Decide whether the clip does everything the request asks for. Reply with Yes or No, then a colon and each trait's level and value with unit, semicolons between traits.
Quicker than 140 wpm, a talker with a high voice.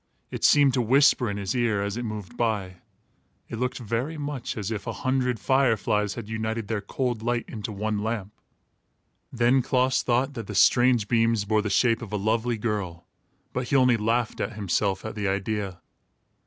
No: average, 190 wpm; low, 115 Hz